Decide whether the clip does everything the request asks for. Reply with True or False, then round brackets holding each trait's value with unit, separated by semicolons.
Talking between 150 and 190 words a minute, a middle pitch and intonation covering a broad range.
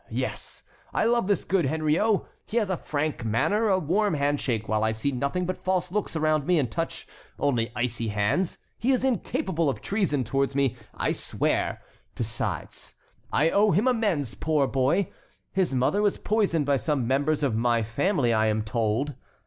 True (175 wpm; 150 Hz; 7.3 semitones)